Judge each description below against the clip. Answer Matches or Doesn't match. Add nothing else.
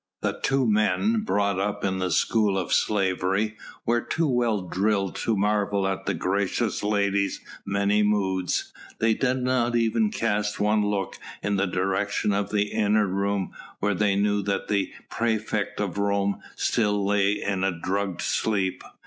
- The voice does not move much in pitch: Matches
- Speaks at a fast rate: Doesn't match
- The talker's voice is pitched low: Matches